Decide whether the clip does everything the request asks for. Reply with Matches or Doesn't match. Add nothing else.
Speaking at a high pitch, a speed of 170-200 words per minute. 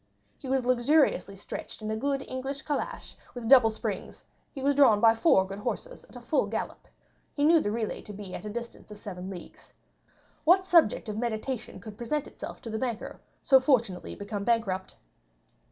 Matches